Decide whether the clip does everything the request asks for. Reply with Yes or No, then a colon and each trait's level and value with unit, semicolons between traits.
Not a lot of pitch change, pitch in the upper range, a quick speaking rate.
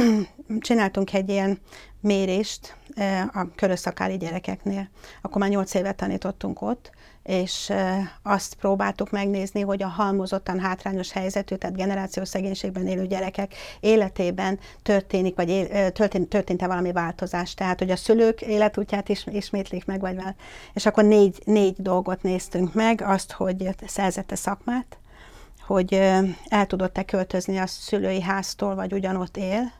No: narrow, 1.4 semitones; high, 195 Hz; average, 135 wpm